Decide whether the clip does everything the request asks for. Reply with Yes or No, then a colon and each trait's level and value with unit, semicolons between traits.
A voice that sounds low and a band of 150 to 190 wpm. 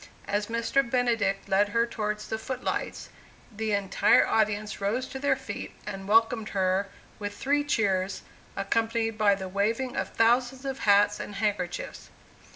No: high, 215 Hz; average, 155 wpm